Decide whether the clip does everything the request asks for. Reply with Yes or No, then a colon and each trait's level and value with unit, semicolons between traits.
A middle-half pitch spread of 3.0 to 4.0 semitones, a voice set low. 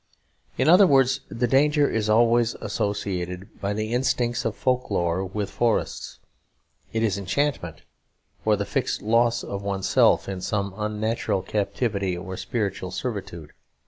Yes: average, 3.6 semitones; low, 105 Hz